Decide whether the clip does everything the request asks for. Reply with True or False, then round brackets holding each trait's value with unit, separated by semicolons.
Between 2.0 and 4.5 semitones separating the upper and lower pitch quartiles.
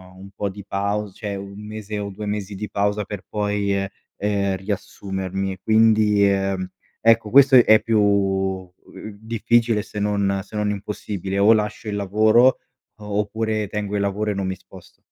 False (1.5 semitones)